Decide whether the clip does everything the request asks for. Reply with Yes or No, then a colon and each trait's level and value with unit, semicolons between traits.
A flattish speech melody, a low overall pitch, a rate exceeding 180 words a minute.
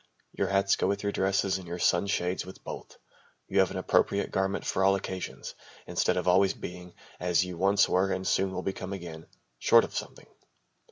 Yes: narrow, 1.3 semitones; very low, 95 Hz; average, 190 wpm